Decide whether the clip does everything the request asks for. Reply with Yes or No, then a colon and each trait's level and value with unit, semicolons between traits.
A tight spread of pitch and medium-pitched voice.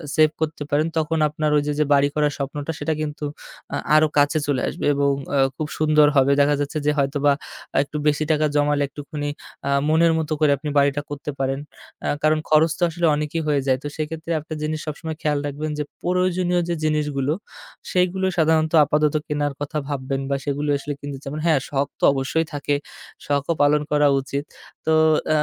Yes: narrow, 1.5 semitones; medium, 150 Hz